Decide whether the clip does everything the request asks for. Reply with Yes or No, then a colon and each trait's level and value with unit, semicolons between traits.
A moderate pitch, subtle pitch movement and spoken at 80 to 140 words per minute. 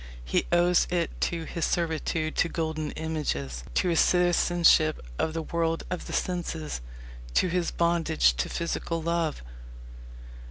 Yes: medium, 165 Hz; narrow, 1.6 semitones; slow, 135 wpm